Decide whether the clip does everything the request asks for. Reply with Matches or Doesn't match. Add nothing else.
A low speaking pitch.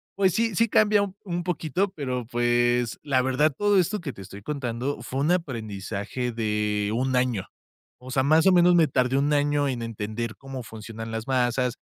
Matches